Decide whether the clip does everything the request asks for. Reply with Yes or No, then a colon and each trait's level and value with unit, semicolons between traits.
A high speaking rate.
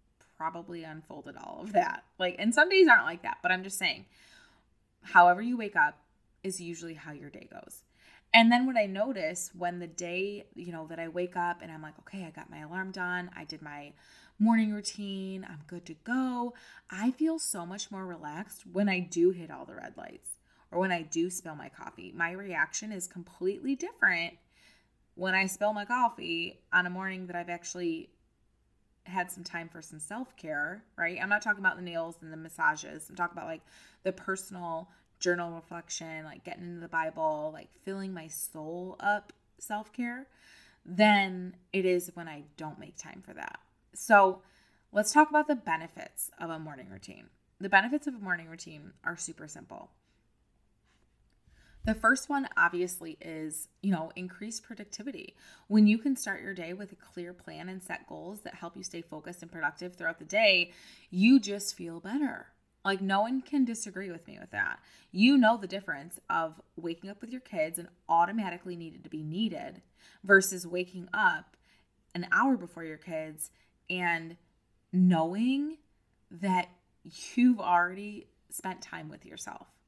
No: average, 180 wpm